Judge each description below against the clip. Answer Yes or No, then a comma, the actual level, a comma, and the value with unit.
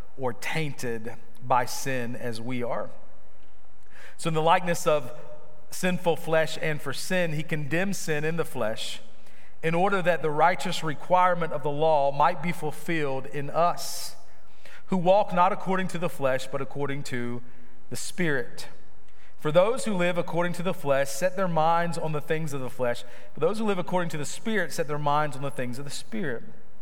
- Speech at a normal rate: Yes, average, 185 wpm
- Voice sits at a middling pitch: Yes, medium, 155 Hz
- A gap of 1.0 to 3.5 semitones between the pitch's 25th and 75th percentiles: No, average, 4.5 semitones